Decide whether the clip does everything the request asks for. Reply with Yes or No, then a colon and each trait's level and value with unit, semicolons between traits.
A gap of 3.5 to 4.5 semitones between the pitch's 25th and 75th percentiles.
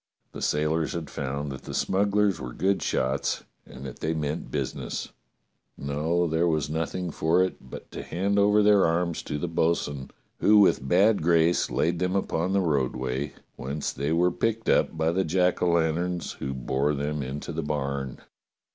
Yes: average, 4.0 semitones